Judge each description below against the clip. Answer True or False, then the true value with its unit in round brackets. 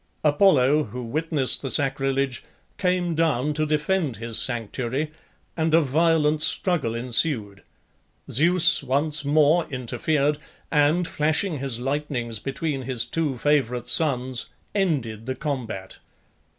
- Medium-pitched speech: True (145 Hz)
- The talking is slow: True (115 wpm)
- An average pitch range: True (3.9 semitones)